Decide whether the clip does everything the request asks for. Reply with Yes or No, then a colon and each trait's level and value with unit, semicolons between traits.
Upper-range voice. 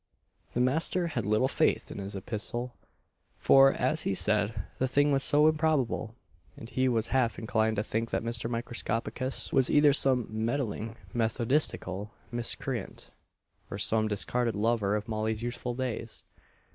No: low, 120 Hz